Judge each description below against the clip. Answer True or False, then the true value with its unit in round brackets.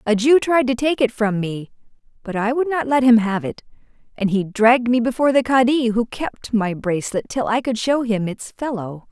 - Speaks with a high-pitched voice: True (235 Hz)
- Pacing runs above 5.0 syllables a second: True (5.2 syllables/s)